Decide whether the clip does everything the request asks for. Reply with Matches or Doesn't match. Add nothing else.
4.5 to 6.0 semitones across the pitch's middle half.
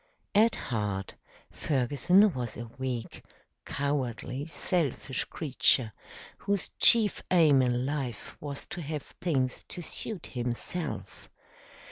Matches